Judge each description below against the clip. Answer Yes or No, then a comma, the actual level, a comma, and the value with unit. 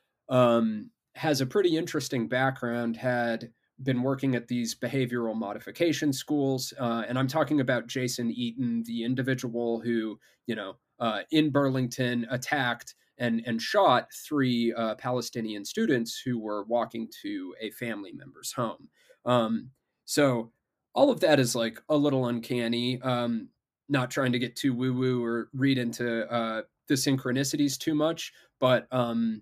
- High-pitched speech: No, low, 125 Hz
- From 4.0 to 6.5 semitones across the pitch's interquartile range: No, average, 2.7 semitones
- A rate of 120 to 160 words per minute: Yes, average, 145 wpm